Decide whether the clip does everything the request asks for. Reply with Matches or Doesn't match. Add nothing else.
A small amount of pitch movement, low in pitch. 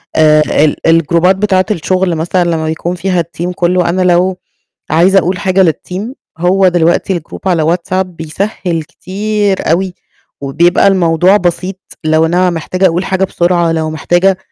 Doesn't match